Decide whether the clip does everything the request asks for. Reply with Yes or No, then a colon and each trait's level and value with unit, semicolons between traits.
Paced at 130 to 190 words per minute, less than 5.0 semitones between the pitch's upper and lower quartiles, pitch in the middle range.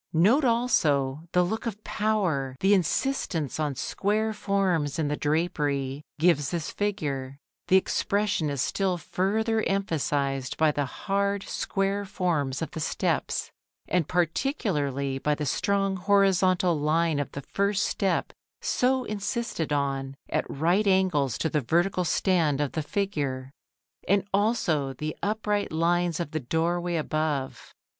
No: slow, 135 wpm; average, 5.3 semitones; medium, 170 Hz